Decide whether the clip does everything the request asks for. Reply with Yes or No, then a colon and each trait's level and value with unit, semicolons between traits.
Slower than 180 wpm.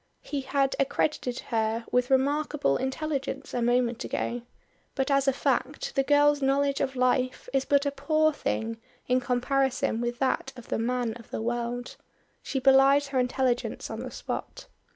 Yes: average, 165 wpm